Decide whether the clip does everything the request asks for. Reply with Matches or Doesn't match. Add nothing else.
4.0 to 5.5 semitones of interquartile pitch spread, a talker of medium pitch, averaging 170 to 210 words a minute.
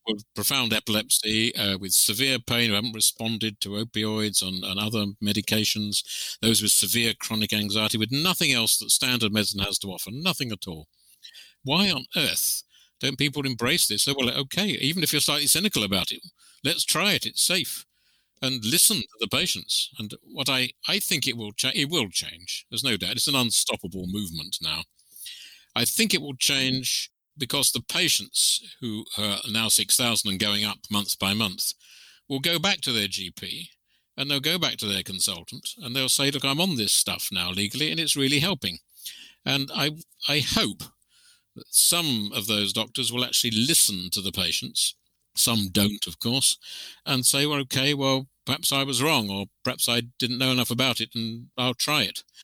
Doesn't match